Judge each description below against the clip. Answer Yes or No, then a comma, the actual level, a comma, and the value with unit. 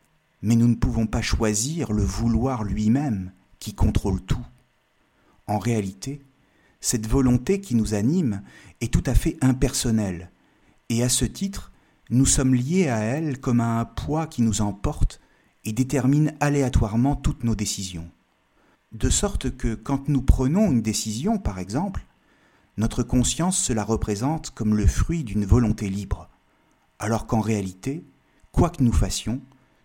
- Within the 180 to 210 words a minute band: No, average, 150 wpm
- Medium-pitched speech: No, low, 115 Hz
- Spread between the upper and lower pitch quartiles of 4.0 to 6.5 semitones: Yes, average, 4.3 semitones